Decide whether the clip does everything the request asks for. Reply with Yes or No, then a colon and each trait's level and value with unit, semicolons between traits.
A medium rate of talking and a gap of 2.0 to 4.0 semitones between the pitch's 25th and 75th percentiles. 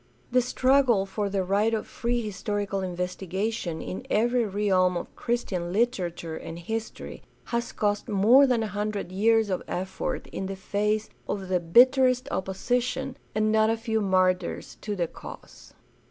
Yes: average, 155 wpm; average, 3.7 semitones